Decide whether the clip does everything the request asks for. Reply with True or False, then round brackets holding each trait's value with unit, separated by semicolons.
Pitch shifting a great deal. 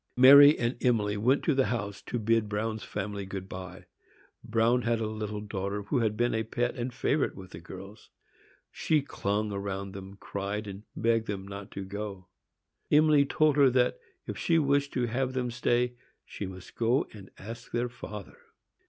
False (3.6 semitones)